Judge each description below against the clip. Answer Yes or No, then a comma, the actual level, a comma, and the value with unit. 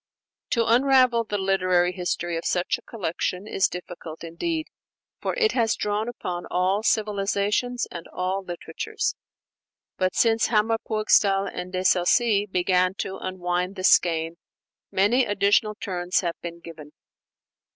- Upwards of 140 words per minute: No, slow, 135 wpm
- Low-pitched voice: No, high, 195 Hz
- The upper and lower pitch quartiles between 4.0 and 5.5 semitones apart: No, average, 3.4 semitones